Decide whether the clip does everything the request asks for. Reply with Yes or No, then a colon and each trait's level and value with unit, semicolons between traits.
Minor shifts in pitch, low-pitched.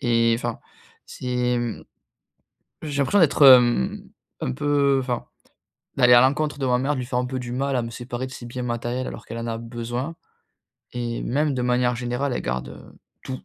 Yes: narrow, 1.9 semitones; low, 125 Hz